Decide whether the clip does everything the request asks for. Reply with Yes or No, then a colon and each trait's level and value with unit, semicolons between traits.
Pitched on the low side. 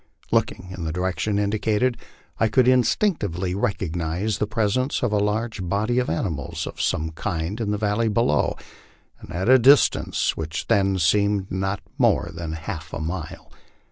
Yes: low, 100 Hz